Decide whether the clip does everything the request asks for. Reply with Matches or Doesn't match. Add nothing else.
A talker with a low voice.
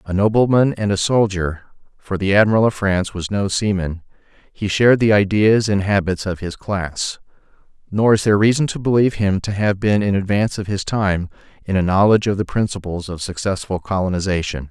Matches